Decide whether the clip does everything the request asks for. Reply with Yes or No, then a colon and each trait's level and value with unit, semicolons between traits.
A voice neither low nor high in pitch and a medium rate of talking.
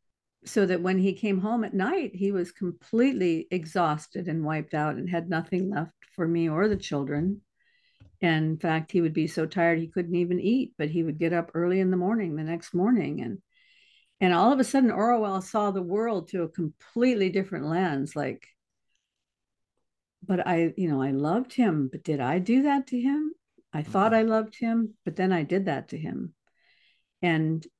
Yes: medium, 180 Hz; average, 195 wpm